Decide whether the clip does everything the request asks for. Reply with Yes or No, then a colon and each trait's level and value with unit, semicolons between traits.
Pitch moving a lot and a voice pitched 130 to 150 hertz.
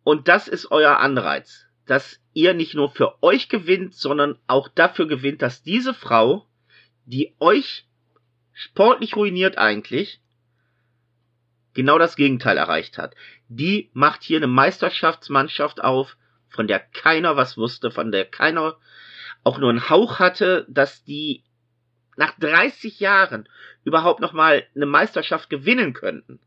Yes: wide, 5.9 semitones; medium, 140 Hz